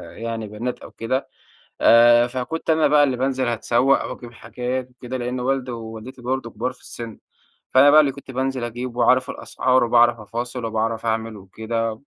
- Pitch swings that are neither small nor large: No, narrow, 2.1 semitones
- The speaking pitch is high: No, low, 120 Hz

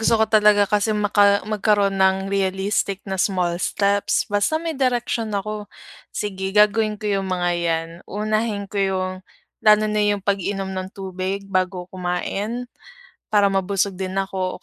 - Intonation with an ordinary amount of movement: No, narrow, 1.7 semitones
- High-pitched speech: Yes, high, 200 Hz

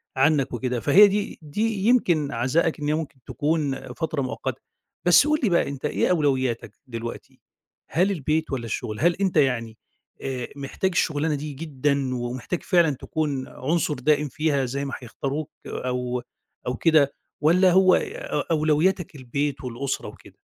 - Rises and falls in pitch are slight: No, average, 4.1 semitones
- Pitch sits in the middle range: Yes, medium, 145 Hz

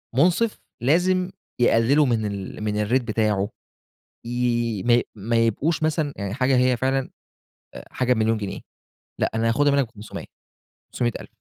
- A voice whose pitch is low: Yes, low, 120 Hz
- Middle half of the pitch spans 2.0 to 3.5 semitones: No, average, 3.9 semitones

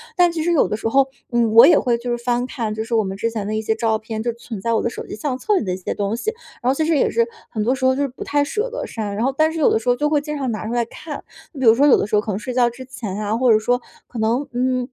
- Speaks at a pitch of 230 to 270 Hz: Yes, high, 240 Hz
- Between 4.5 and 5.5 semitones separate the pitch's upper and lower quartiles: No, average, 3.7 semitones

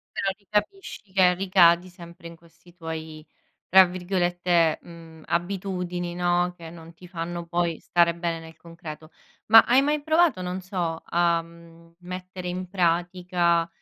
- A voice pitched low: No, medium, 175 Hz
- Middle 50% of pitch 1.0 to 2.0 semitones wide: Yes, narrow, 1.5 semitones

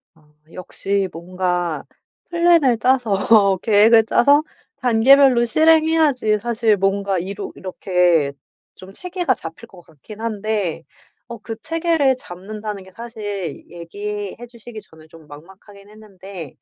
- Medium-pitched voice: No, high, 210 Hz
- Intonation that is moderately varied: Yes, average, 4.5 semitones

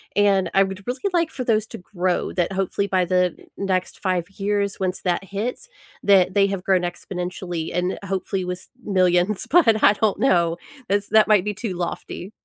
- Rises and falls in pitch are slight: Yes, narrow, 2.2 semitones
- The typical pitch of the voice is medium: No, high, 195 Hz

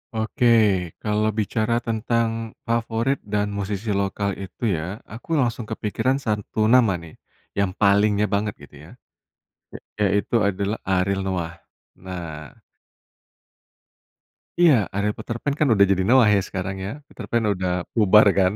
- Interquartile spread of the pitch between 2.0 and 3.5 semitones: Yes, average, 2.8 semitones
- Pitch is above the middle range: No, low, 105 Hz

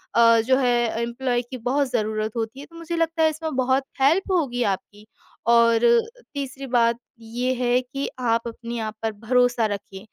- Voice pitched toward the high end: Yes, high, 245 Hz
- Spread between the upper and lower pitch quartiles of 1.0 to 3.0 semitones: Yes, average, 2.7 semitones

